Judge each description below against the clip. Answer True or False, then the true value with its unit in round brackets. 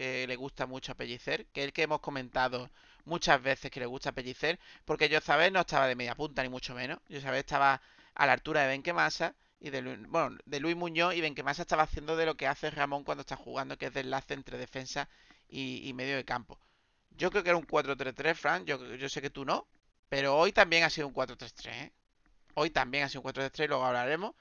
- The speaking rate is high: True (230 wpm)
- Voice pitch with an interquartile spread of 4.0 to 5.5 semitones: False (2.9 semitones)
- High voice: False (140 Hz)